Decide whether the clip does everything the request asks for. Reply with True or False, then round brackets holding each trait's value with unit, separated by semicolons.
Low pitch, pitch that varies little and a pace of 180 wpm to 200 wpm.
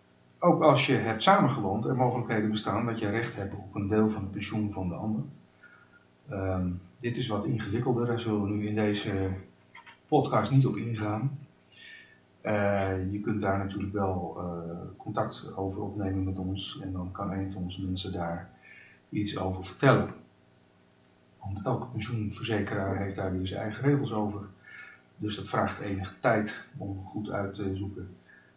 False (100 Hz; 2.3 semitones; 165 wpm)